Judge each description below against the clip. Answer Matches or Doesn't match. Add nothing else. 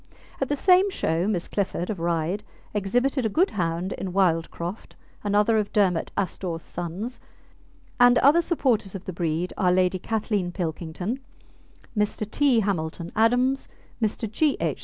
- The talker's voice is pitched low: Doesn't match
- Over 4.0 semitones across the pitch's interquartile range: Matches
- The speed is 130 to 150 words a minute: Matches